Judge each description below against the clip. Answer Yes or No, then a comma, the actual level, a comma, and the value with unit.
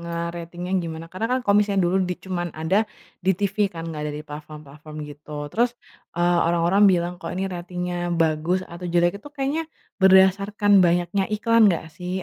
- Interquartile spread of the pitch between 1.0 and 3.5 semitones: Yes, narrow, 2.6 semitones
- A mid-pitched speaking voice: Yes, medium, 175 Hz